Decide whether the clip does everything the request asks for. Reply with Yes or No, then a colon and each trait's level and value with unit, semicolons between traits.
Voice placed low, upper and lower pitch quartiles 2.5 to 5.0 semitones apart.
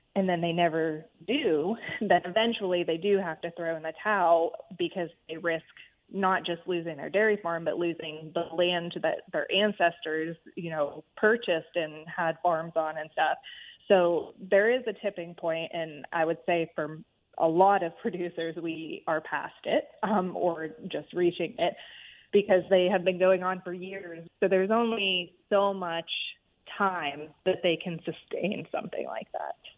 No: medium, 175 Hz; average, 2.8 semitones